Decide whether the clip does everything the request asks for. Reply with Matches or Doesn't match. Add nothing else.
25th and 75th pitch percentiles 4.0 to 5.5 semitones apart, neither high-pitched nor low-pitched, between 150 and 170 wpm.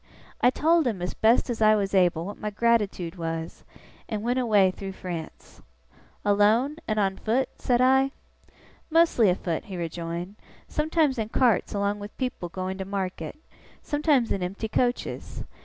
Doesn't match